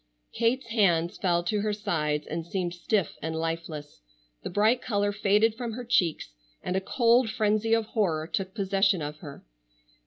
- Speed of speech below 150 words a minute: No, average, 165 wpm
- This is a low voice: No, high, 195 Hz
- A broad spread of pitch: No, average, 4.8 semitones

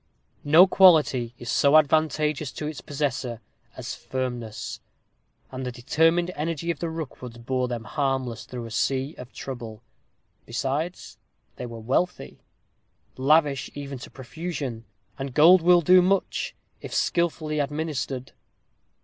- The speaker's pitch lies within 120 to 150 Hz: Yes, medium, 140 Hz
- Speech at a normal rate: No, slow, 130 wpm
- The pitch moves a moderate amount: Yes, average, 4.1 semitones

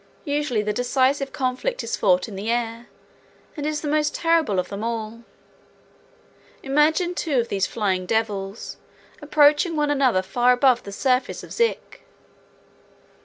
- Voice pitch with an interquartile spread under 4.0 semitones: No, wide, 5.6 semitones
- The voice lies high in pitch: Yes, very high, 250 Hz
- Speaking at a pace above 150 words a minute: No, average, 145 wpm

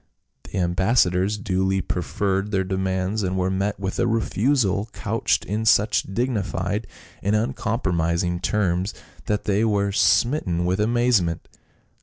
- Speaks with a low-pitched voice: Yes, low, 100 Hz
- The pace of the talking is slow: Yes, slow, 130 wpm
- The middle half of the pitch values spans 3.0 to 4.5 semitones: No, narrow, 2.5 semitones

